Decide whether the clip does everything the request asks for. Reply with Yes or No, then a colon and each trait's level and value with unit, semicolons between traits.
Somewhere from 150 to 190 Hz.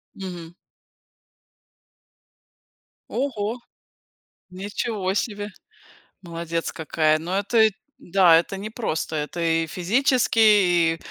Yes: medium, 185 Hz